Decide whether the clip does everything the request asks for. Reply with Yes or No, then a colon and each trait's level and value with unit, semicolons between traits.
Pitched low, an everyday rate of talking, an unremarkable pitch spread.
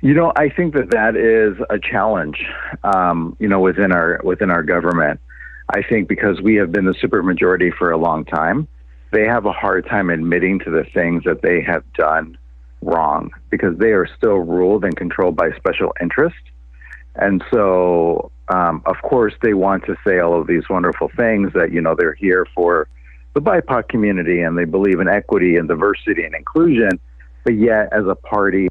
Yes: very low, 90 Hz; average, 190 wpm; average, 3.6 semitones